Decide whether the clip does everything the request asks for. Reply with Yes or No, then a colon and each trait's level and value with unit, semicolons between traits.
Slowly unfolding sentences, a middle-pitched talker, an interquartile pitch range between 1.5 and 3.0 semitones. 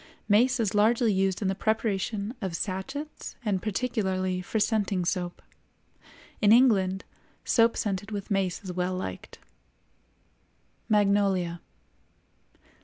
No: slow, 110 wpm; high, 200 Hz; average, 2.7 semitones